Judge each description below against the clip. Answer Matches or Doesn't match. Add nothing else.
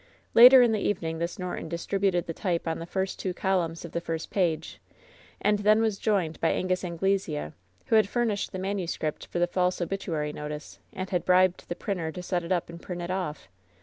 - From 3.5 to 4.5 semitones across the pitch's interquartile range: Doesn't match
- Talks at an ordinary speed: Doesn't match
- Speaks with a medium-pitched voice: Matches